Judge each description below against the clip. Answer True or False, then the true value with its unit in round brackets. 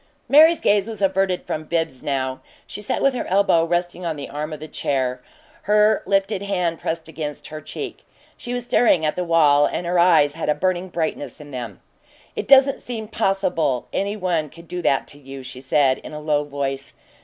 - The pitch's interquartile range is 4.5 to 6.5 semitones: True (5.1 semitones)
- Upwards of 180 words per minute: True (200 wpm)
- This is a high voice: False (165 Hz)